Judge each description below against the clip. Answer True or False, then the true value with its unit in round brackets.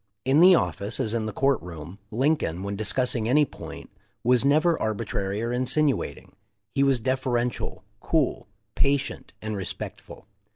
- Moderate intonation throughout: True (4.5 semitones)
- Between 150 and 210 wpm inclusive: False (140 wpm)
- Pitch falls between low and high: False (125 Hz)